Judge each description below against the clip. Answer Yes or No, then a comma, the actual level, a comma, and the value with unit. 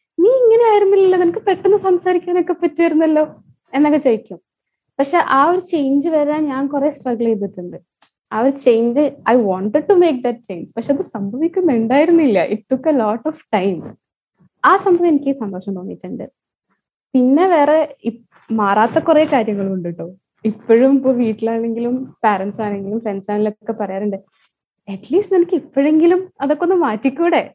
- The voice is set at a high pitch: Yes, very high, 275 Hz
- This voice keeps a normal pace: No, fast, 135 wpm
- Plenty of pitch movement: Yes, wide, 7.3 semitones